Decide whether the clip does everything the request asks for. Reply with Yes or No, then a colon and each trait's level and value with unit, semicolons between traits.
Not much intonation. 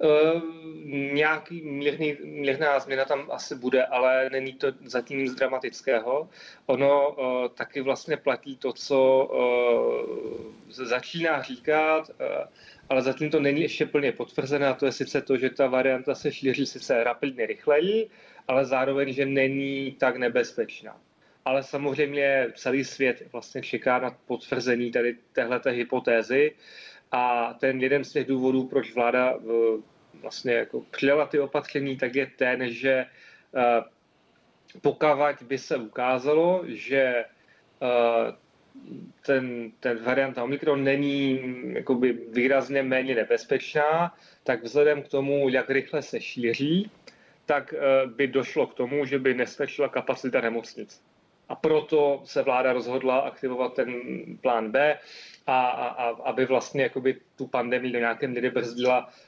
Yes: narrow, 2.2 semitones